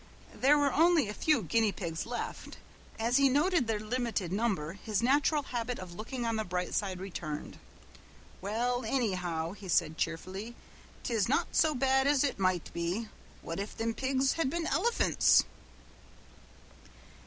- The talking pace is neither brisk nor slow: Yes, average, 155 wpm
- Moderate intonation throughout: No, wide, 6.2 semitones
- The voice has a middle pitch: No, high, 225 Hz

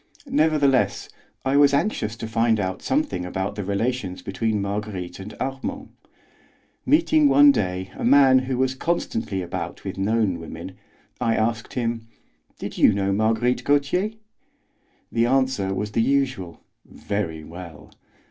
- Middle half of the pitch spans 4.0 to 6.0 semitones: Yes, wide, 5.6 semitones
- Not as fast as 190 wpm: Yes, average, 140 wpm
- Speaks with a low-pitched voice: Yes, low, 115 Hz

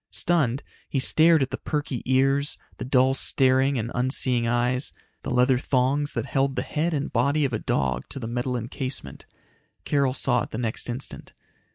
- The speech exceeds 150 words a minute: Yes, average, 180 wpm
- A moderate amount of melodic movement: No, narrow, 2.2 semitones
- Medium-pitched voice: No, low, 130 Hz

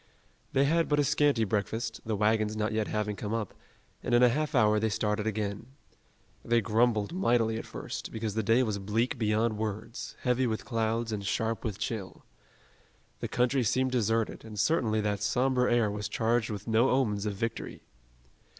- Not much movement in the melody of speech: Yes, narrow, 2.2 semitones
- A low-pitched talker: Yes, low, 110 Hz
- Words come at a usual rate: Yes, average, 180 wpm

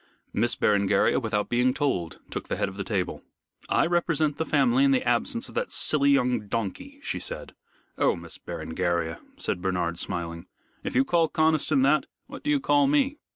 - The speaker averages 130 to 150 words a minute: No, average, 185 wpm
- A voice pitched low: Yes, low, 130 Hz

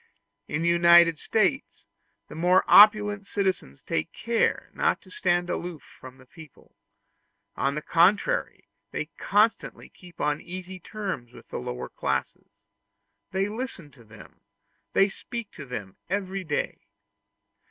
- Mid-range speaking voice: Yes, medium, 175 Hz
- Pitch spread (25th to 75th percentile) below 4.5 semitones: No, average, 5.2 semitones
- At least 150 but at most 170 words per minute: No, average, 140 wpm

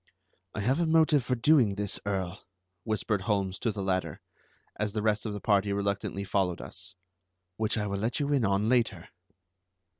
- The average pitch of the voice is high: No, low, 105 Hz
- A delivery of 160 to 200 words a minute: Yes, average, 180 wpm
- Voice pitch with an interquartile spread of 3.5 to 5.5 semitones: No, narrow, 2.6 semitones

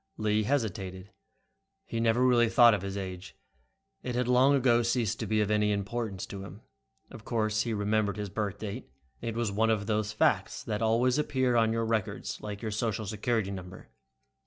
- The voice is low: Yes, low, 110 Hz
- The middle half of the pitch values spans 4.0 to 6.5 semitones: No, narrow, 2.4 semitones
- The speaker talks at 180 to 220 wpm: Yes, average, 185 wpm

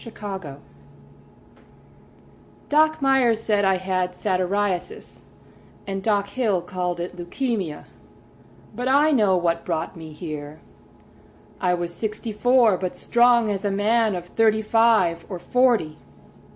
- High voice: Yes, high, 200 Hz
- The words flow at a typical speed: No, slow, 125 wpm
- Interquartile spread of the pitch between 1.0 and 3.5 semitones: No, average, 4.4 semitones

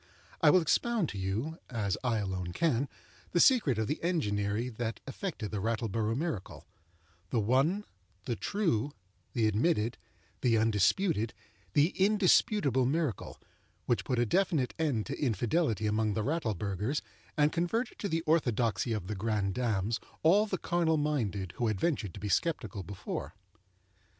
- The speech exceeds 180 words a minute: No, average, 140 wpm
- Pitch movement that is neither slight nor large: No, wide, 7.4 semitones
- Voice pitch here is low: Yes, low, 120 Hz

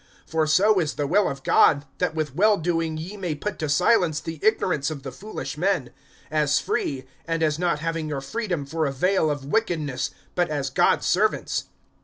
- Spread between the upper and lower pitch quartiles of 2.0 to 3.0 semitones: No, average, 3.8 semitones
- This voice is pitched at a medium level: Yes, medium, 160 Hz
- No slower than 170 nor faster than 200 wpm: Yes, average, 195 wpm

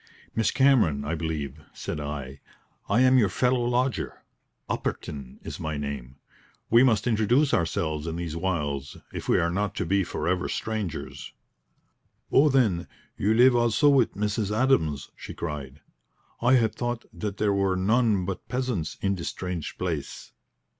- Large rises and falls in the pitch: Yes, wide, 7.3 semitones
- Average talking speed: Yes, average, 155 wpm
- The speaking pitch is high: No, very low, 95 Hz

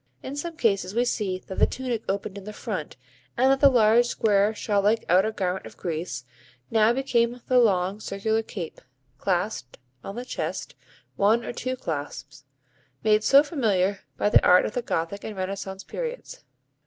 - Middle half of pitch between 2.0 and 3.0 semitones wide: No, average, 4.1 semitones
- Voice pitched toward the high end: Yes, high, 210 Hz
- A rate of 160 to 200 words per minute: Yes, average, 175 wpm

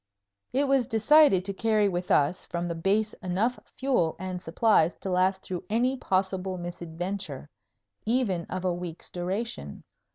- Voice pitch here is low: No, high, 190 Hz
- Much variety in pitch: No, average, 3.9 semitones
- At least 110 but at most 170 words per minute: Yes, average, 150 wpm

